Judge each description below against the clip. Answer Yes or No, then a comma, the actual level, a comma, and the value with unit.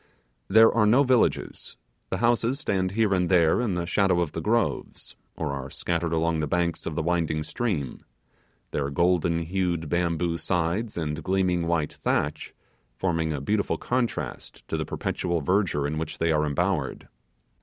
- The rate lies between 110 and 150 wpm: No, average, 165 wpm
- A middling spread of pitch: Yes, average, 3.4 semitones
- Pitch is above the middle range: No, very low, 85 Hz